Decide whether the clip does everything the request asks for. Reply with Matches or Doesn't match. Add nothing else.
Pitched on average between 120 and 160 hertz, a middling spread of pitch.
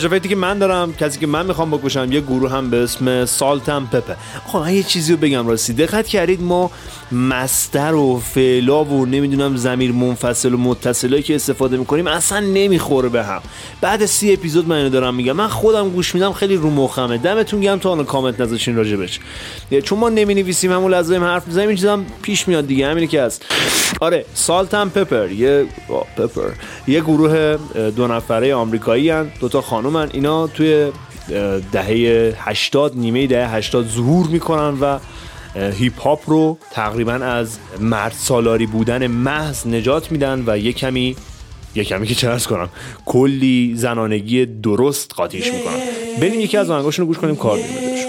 Doesn't match